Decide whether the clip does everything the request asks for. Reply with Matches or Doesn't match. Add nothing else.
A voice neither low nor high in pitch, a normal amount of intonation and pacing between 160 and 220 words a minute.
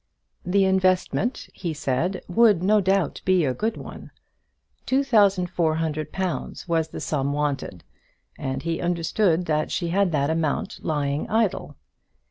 Doesn't match